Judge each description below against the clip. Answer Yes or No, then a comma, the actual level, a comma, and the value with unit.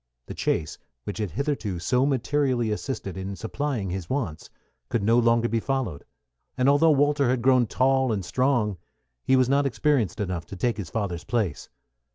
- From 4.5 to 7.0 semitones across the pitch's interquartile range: Yes, average, 5.3 semitones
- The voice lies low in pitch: Yes, low, 120 Hz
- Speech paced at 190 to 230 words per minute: No, average, 175 wpm